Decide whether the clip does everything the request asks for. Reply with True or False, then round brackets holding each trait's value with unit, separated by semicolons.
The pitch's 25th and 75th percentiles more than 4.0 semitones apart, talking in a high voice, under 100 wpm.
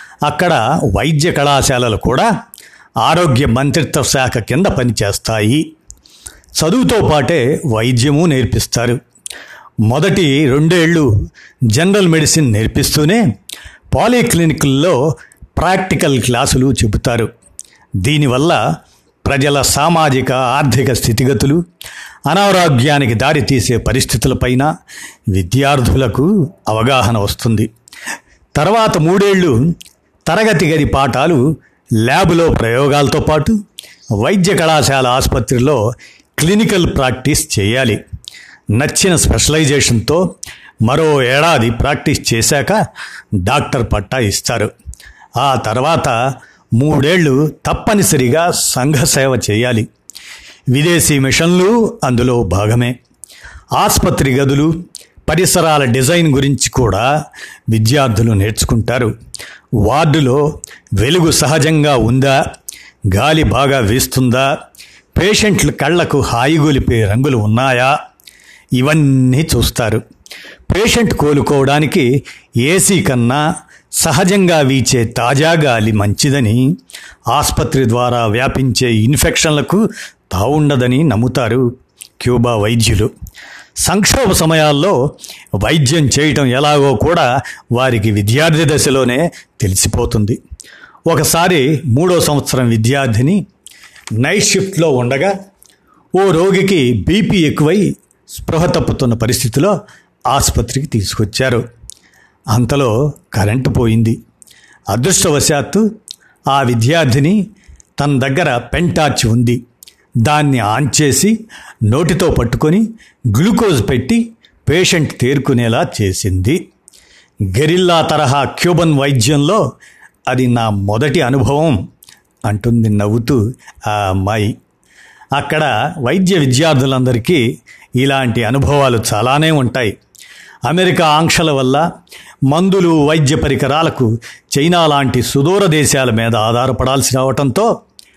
False (4.7 semitones; 135 Hz; 80 wpm)